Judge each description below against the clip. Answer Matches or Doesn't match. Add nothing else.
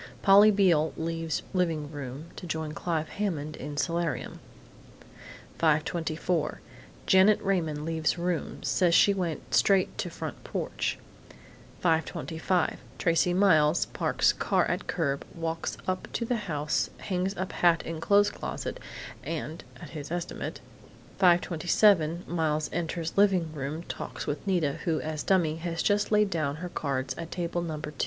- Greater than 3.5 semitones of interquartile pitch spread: Doesn't match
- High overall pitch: Doesn't match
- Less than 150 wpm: Matches